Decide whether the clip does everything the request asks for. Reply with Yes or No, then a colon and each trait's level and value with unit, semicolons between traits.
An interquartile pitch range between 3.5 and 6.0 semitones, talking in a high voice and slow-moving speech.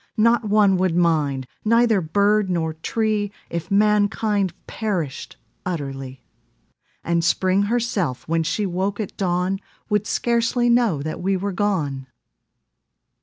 Yes: average, 4.3 semitones; high, 195 Hz; slow, 120 wpm